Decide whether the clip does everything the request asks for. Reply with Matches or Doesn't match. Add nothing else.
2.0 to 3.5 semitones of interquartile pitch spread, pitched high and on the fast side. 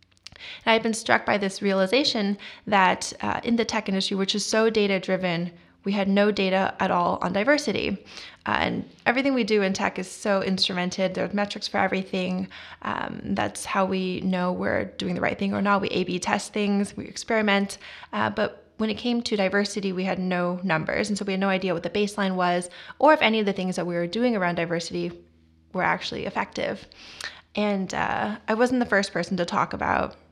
Matches